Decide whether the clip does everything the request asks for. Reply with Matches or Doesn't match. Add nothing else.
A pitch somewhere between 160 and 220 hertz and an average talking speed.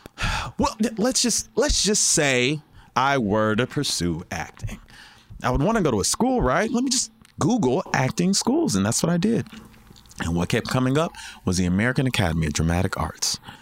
Doesn't match